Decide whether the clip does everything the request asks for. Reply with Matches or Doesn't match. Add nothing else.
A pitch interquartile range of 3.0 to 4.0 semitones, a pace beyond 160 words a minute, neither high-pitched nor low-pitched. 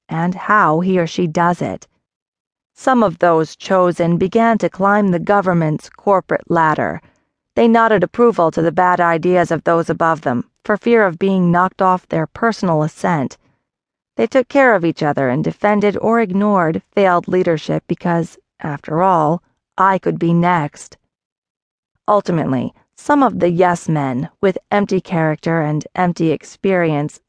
Doesn't match